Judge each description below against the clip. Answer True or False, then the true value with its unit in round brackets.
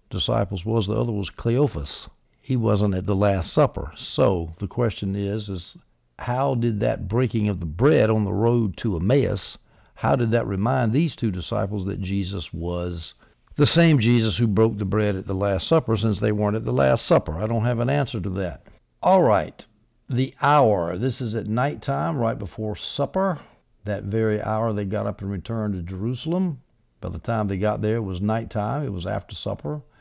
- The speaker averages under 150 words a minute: False (195 wpm)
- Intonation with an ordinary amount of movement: True (3.2 semitones)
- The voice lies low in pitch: True (105 Hz)